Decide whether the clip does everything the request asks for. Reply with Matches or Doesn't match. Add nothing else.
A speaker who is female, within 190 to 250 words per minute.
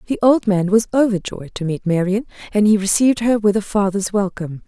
Matches